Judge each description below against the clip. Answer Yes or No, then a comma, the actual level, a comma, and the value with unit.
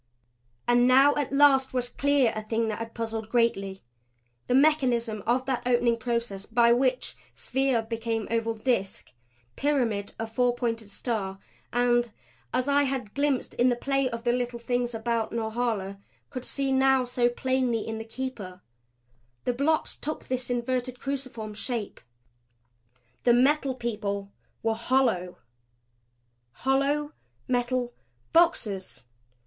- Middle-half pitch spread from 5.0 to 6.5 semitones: No, average, 2.7 semitones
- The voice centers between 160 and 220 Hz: No, high, 240 Hz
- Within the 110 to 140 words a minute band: Yes, slow, 135 wpm